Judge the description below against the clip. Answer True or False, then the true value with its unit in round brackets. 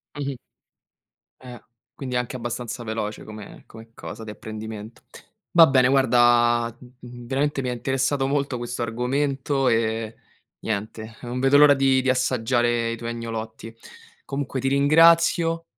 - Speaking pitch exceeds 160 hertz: False (125 Hz)